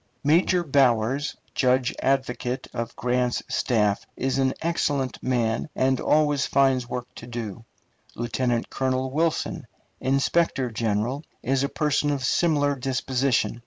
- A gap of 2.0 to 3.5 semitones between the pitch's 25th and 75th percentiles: Yes, narrow, 2.5 semitones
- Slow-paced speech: Yes, slow, 125 wpm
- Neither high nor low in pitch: No, low, 130 Hz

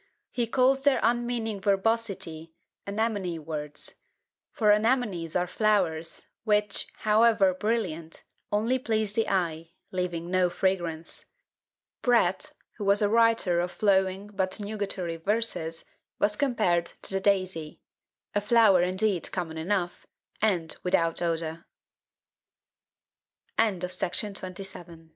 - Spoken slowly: Yes, slow, 105 wpm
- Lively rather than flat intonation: No, average, 4.1 semitones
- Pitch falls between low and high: No, high, 195 Hz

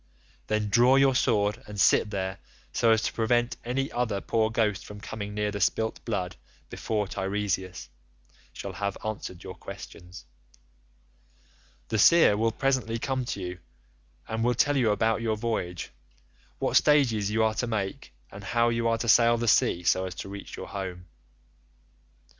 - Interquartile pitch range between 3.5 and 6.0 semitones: No, average, 3.0 semitones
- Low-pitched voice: Yes, low, 110 Hz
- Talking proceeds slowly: No, average, 165 wpm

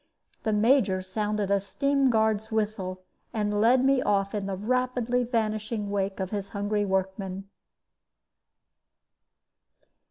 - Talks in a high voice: Yes, high, 210 Hz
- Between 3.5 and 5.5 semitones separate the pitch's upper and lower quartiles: No, narrow, 2.5 semitones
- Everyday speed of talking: No, slow, 120 wpm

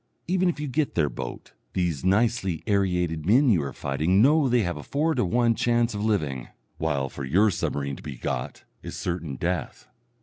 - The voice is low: Yes, very low, 95 Hz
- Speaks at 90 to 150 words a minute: No, average, 195 wpm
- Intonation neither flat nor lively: No, wide, 7.9 semitones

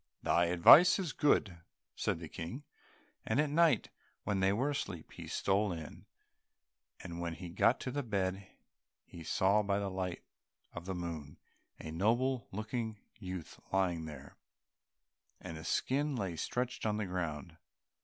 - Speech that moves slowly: No, average, 155 wpm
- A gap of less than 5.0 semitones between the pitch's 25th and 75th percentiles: No, wide, 5.4 semitones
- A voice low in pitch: Yes, very low, 95 Hz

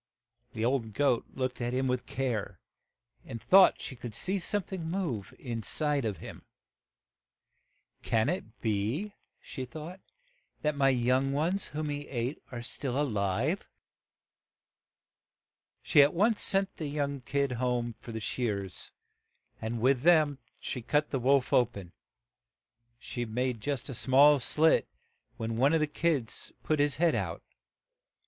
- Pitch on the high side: No, low, 135 Hz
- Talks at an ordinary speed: Yes, average, 155 wpm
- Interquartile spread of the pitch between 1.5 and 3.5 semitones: No, average, 4.2 semitones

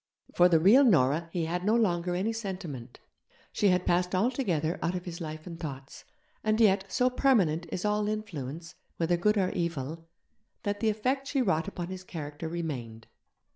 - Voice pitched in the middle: Yes, medium, 180 Hz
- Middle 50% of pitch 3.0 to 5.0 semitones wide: Yes, average, 4.4 semitones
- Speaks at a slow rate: No, average, 175 wpm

